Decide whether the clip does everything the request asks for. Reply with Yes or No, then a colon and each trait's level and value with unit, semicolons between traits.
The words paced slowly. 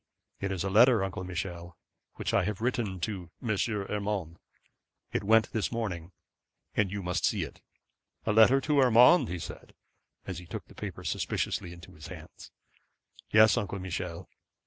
No: average, 165 wpm